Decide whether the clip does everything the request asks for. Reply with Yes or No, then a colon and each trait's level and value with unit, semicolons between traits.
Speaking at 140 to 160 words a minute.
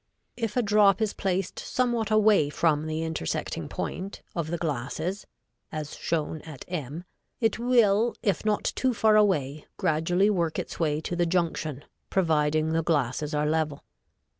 Yes: average, 155 wpm